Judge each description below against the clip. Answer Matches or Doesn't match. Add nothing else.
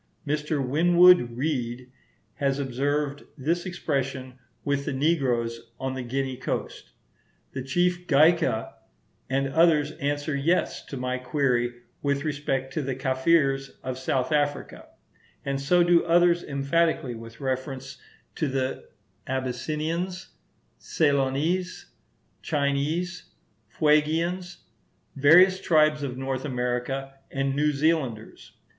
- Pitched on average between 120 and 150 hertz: Matches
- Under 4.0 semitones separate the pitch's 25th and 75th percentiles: Matches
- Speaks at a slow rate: Matches